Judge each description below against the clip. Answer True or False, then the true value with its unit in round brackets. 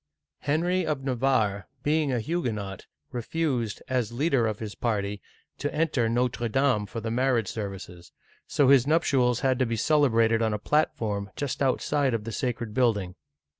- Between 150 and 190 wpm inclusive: True (165 wpm)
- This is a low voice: True (120 Hz)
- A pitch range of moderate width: True (4.2 semitones)